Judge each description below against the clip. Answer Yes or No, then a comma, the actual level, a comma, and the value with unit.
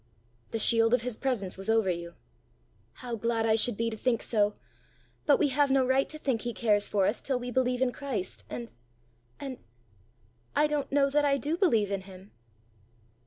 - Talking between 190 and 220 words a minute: Yes, average, 195 wpm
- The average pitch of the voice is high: Yes, high, 240 Hz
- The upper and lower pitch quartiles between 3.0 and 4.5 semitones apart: Yes, average, 4.1 semitones